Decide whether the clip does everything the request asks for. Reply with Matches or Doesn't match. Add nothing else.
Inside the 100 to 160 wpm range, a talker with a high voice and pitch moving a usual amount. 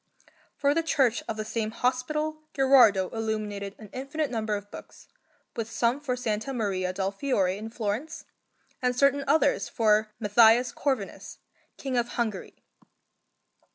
Matches